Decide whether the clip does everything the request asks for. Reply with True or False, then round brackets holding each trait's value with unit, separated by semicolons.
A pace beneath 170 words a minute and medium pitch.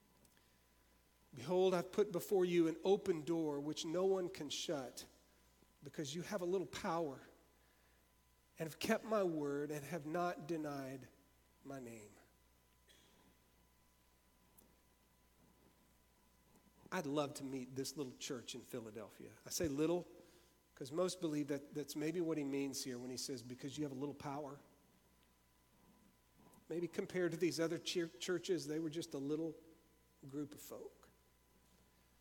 True (140 wpm; 145 Hz)